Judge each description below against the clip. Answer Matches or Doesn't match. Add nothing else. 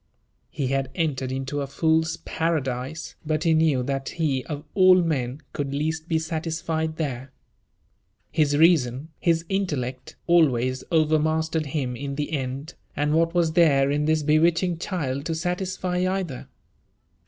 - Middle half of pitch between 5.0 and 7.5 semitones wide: Doesn't match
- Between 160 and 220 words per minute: Doesn't match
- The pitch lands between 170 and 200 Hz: Doesn't match